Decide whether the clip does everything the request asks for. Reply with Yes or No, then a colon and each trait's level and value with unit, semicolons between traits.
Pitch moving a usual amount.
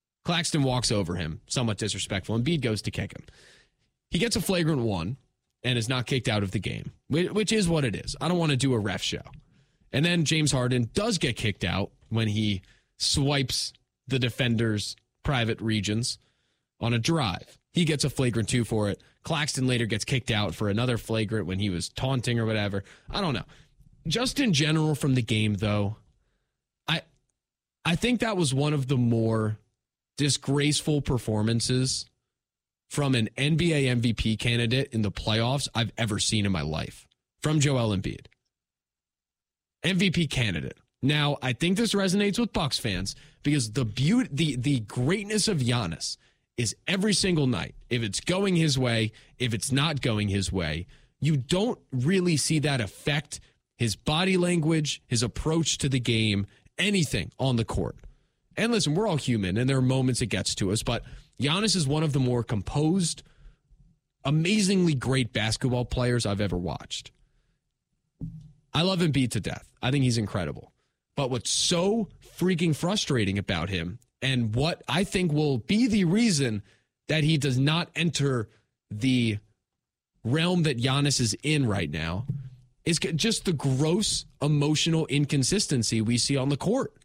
No: wide, 5.7 semitones